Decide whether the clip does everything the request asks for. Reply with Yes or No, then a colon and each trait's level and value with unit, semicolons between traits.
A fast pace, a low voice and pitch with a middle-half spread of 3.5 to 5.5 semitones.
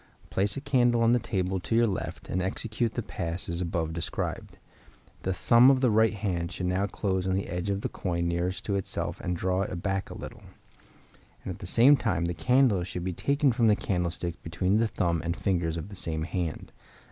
Yes: fast, 220 wpm; very low, 95 Hz; average, 4.4 semitones